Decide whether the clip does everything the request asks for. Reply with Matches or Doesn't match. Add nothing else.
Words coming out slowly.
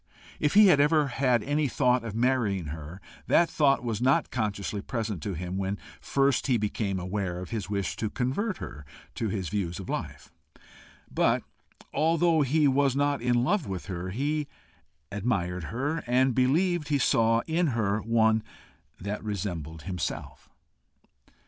Doesn't match